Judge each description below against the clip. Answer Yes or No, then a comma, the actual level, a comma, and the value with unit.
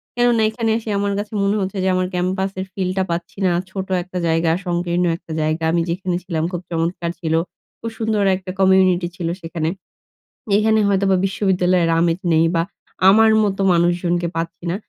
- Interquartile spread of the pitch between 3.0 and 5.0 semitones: No, narrow, 2.4 semitones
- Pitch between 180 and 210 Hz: Yes, medium, 185 Hz